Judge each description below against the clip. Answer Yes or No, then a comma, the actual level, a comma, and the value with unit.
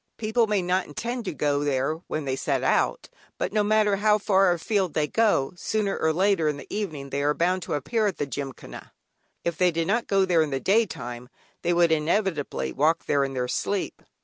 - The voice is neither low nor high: Yes, medium, 170 Hz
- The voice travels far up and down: Yes, wide, 5.9 semitones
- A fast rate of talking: Yes, fast, 210 wpm